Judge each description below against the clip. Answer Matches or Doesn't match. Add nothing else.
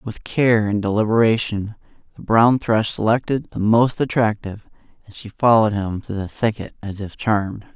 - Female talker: Doesn't match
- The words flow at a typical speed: Matches